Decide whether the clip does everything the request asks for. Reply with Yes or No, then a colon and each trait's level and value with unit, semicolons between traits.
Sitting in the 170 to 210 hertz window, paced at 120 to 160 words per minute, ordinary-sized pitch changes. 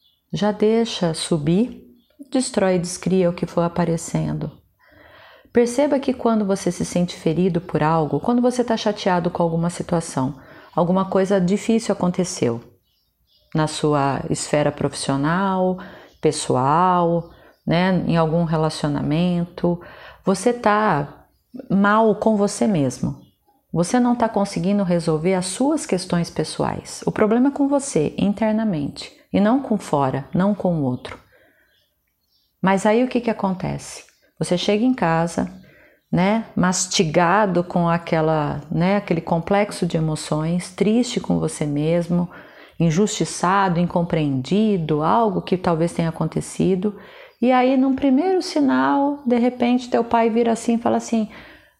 Yes: medium, 185 Hz; average, 130 wpm; average, 4.8 semitones